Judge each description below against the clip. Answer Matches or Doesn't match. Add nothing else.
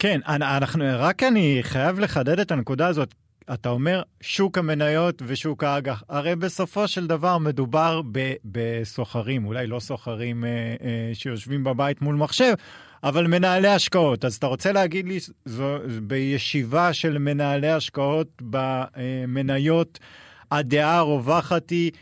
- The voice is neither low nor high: Matches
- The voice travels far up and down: Doesn't match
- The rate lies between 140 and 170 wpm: Doesn't match